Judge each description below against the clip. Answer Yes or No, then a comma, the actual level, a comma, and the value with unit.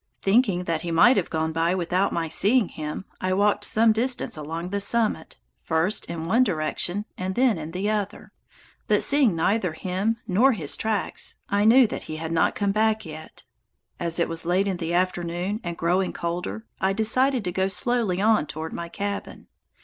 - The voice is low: No, medium, 185 Hz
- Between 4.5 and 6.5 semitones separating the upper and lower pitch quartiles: No, average, 4.1 semitones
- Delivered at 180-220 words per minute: Yes, average, 185 wpm